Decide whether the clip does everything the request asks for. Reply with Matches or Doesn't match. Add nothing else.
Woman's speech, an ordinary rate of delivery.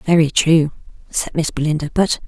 Matches